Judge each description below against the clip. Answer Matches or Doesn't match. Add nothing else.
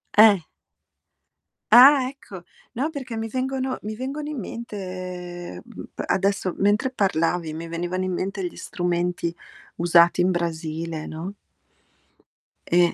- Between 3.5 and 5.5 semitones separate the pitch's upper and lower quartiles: Matches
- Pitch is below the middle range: Doesn't match